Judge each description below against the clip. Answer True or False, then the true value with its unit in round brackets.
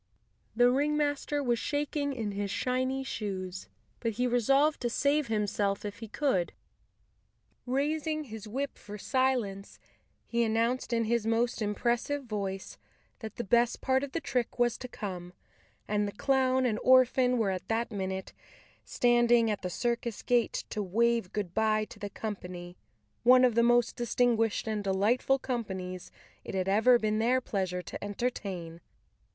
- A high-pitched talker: True (230 Hz)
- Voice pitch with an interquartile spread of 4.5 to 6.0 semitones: False (3.7 semitones)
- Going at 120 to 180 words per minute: True (155 wpm)